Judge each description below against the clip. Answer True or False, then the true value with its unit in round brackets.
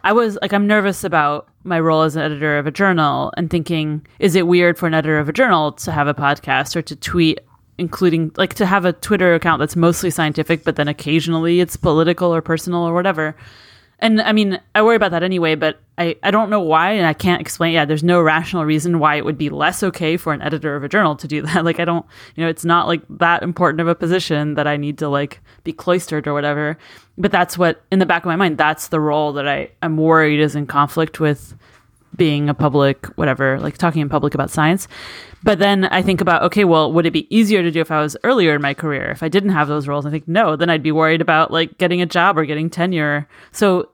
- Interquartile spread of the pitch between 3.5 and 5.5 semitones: False (2.8 semitones)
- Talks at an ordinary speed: False (250 wpm)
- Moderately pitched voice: True (165 Hz)